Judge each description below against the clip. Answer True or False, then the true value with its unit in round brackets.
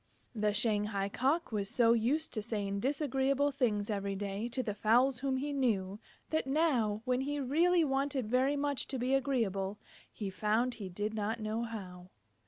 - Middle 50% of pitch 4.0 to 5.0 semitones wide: True (4.6 semitones)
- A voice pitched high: True (235 Hz)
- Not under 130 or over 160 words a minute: False (175 wpm)